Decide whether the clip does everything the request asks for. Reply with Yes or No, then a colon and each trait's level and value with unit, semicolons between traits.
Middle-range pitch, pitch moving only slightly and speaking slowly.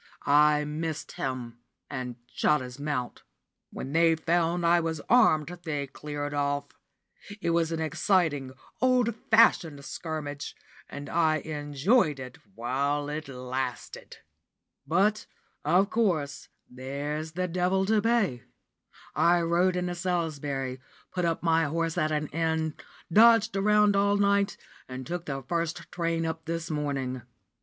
No: medium, 160 Hz; average, 3.6 semitones; slow, 130 wpm